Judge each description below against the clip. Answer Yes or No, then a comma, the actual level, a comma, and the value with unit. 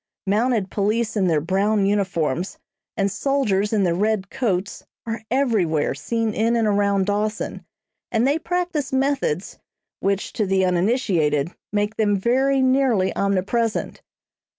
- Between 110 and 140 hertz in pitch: No, high, 210 Hz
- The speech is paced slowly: Yes, slow, 130 wpm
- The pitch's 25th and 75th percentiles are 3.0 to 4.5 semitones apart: Yes, average, 3.7 semitones